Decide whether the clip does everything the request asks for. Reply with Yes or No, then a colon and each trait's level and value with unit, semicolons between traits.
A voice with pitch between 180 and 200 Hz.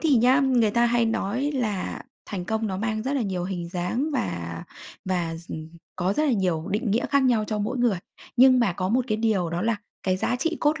No: high, 215 Hz